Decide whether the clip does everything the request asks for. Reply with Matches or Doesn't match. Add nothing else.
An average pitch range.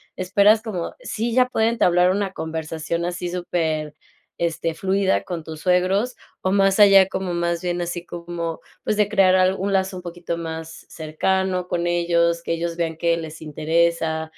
Doesn't match